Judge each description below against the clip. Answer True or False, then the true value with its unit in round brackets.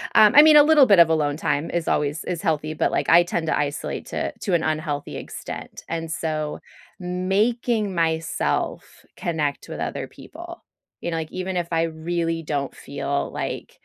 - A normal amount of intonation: True (3.1 semitones)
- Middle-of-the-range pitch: True (165 Hz)